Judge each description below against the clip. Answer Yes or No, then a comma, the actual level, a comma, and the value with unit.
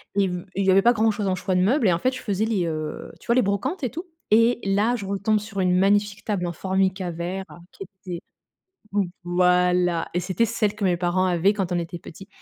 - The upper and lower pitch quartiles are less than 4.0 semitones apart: Yes, average, 2.8 semitones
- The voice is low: No, high, 195 Hz